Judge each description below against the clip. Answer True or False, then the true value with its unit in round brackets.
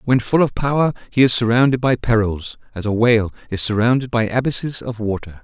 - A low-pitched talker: True (115 Hz)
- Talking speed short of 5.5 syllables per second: False (5.8 syllables/s)